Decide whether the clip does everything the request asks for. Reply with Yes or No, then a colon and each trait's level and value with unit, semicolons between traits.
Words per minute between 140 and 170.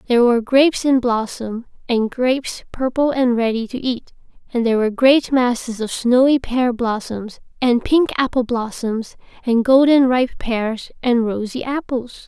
Yes: average, 155 wpm